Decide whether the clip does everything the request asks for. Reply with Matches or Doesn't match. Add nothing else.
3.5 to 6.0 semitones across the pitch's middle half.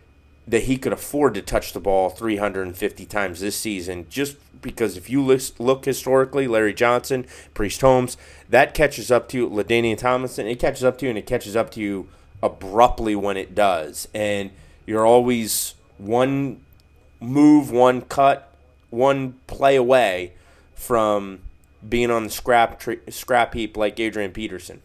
Matches